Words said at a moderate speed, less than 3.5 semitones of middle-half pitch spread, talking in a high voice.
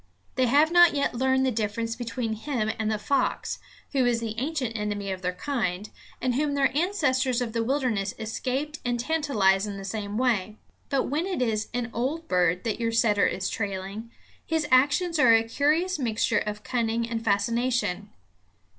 No: average, 180 wpm; average, 4.3 semitones; high, 235 Hz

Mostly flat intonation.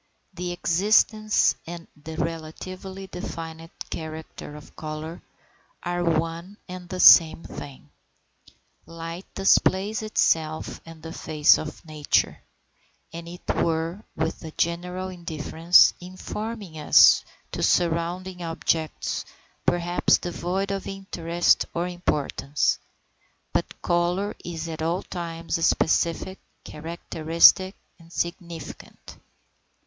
Yes: narrow, 1.9 semitones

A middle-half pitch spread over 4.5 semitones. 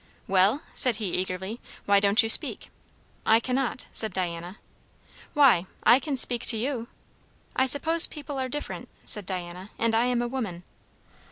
Yes: wide, 5.4 semitones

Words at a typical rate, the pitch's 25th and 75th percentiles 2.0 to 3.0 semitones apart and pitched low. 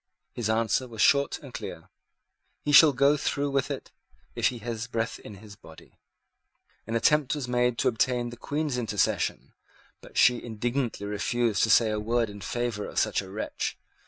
Yes: average, 180 wpm; average, 2.7 semitones; low, 120 Hz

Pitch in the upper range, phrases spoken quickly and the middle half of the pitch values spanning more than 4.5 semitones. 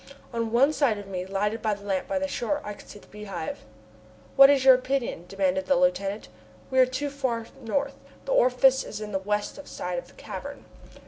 Yes: high, 235 Hz; fast, 210 wpm; average, 5.1 semitones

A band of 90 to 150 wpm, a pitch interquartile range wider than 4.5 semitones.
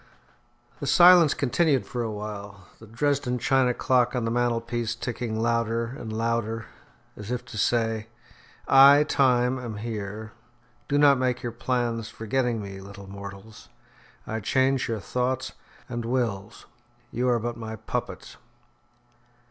No: average, 140 wpm; narrow, 2.4 semitones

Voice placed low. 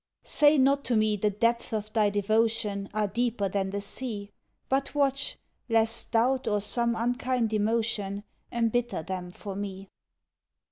No: high, 220 Hz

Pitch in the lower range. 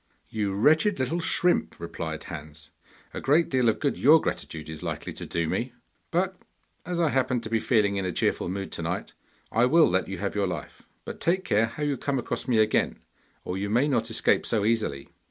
Yes: low, 115 Hz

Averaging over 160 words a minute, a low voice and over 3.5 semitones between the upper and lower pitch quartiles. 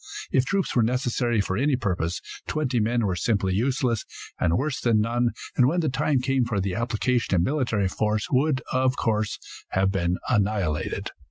Yes: average, 175 wpm; low, 115 Hz; average, 4.3 semitones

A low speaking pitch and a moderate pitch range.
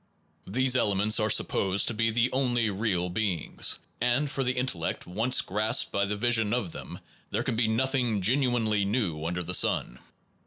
Yes: low, 110 Hz; average, 3.9 semitones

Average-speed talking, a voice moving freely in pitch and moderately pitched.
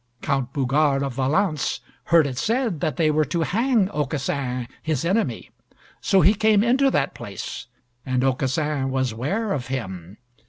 Yes: average, 155 wpm; wide, 6.6 semitones; medium, 150 Hz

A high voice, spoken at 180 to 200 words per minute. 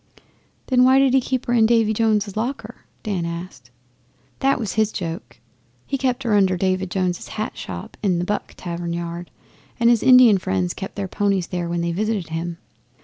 Yes: high, 200 Hz; average, 190 wpm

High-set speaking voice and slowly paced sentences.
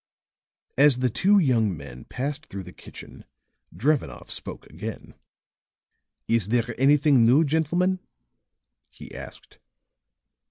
No: low, 125 Hz; slow, 110 wpm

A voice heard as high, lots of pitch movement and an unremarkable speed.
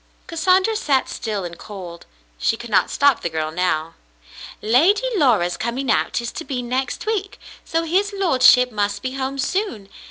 Yes: very high, 255 Hz; wide, 8.4 semitones; average, 165 wpm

